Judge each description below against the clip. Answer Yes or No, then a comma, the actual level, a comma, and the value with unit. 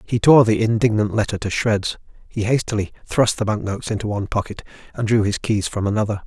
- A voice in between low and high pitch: No, low, 105 Hz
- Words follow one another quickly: Yes, fast, 210 wpm